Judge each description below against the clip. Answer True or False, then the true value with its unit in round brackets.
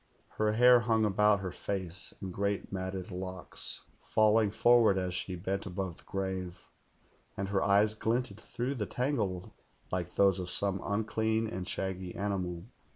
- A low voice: True (100 Hz)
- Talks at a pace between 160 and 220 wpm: True (165 wpm)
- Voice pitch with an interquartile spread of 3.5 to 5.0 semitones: False (2.7 semitones)